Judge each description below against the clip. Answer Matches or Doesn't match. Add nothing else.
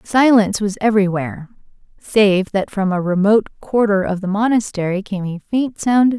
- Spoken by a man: Doesn't match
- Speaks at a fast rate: Doesn't match